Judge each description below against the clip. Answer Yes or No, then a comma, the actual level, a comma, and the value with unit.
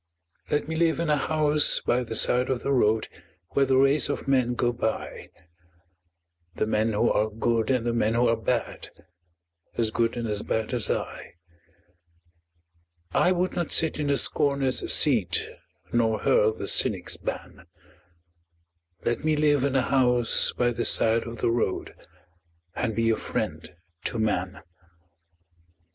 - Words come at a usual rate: Yes, average, 155 wpm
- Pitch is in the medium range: No, low, 120 Hz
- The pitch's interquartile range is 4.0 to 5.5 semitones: No, average, 3.6 semitones